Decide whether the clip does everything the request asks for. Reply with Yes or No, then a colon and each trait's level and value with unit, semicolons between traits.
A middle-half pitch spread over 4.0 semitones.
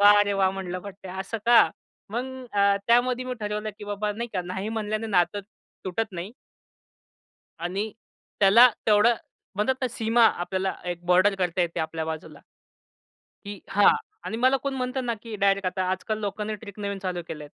No: average, 3.1 semitones